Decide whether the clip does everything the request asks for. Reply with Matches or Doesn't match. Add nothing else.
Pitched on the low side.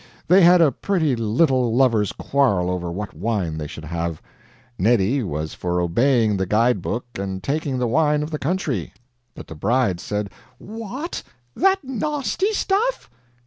Matches